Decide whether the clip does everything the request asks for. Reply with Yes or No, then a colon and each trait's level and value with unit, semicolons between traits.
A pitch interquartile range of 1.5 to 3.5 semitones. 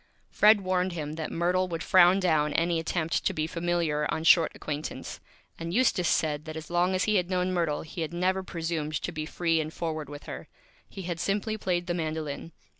Yes: narrow, 2.5 semitones